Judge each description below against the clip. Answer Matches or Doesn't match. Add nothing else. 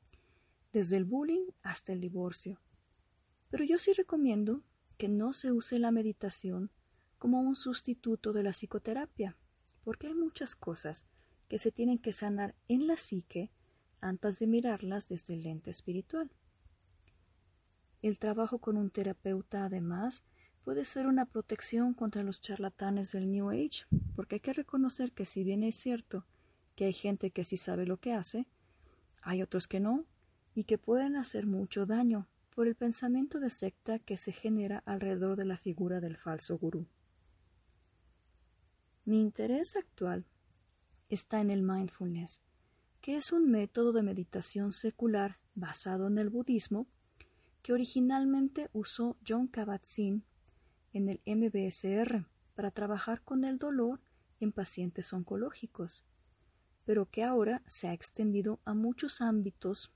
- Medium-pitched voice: Doesn't match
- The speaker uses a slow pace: Doesn't match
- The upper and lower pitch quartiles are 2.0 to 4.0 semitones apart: Doesn't match